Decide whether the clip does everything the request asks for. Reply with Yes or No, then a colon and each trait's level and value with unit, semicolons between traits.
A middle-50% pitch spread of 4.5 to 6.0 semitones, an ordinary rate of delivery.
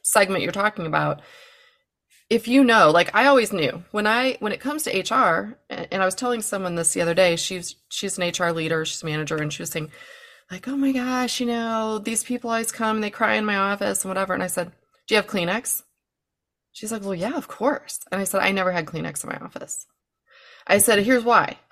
No: average, 5.2 semitones; fast, 230 wpm